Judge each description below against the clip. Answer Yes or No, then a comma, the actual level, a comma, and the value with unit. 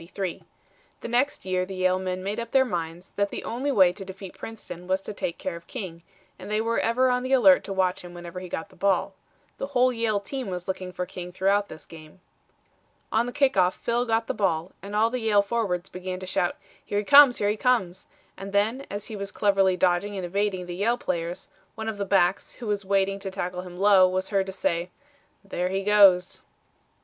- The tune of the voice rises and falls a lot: No, average, 3.2 semitones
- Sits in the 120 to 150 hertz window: No, high, 195 Hz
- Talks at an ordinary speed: No, fast, 225 wpm